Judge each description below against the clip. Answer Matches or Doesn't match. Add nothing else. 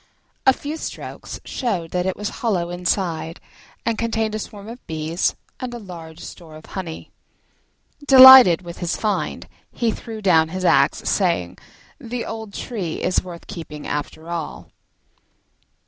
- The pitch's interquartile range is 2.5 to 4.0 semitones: Doesn't match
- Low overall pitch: Doesn't match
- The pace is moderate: Matches